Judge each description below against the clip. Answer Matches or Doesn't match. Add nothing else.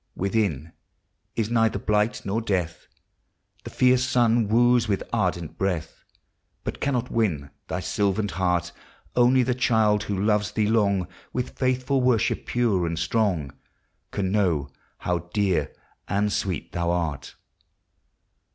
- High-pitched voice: Doesn't match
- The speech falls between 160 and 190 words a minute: Doesn't match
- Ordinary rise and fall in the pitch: Matches